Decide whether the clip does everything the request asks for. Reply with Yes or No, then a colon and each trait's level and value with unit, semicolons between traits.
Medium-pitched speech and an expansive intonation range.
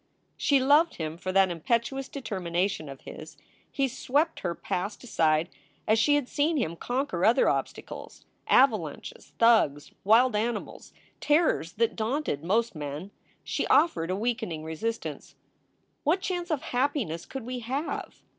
No: high, 225 Hz; wide, 7.9 semitones